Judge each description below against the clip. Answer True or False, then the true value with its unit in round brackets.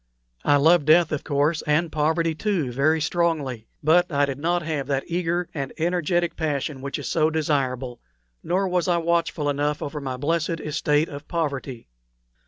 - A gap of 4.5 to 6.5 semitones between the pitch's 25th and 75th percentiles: False (3.0 semitones)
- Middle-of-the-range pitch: True (155 Hz)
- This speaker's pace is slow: False (170 wpm)